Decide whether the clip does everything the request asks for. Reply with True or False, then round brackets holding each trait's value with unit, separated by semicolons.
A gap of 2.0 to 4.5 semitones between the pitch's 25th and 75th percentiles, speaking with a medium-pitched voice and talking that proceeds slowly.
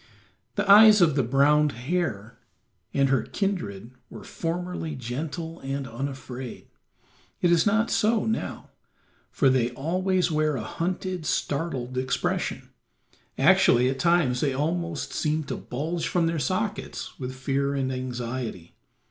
False (5.1 semitones; 145 Hz; 130 wpm)